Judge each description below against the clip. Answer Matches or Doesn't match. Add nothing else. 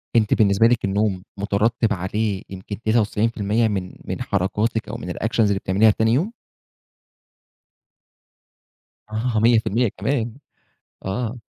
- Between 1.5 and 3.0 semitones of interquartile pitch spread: Matches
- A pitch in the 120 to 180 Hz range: Doesn't match